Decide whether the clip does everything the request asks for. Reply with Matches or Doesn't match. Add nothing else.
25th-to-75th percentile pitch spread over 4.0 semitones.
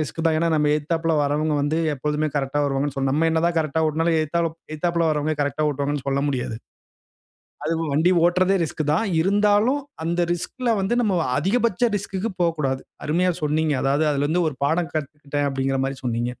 Doesn't match